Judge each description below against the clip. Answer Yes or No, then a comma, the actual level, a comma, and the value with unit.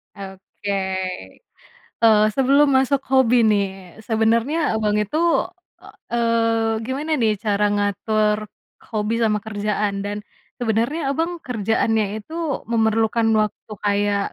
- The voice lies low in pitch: No, high, 220 Hz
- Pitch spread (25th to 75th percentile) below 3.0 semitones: Yes, narrow, 2.4 semitones